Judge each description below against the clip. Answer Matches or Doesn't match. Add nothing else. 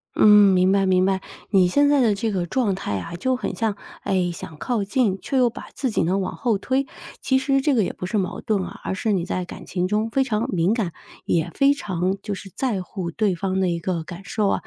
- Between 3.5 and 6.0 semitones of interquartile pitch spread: Matches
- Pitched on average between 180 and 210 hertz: Matches